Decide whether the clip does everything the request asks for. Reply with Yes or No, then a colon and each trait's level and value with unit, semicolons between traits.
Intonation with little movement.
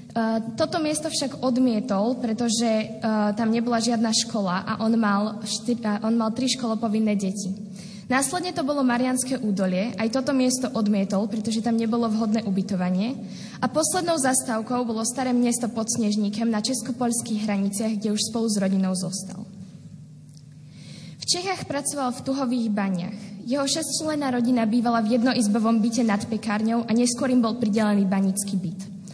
No: average, 3.4 semitones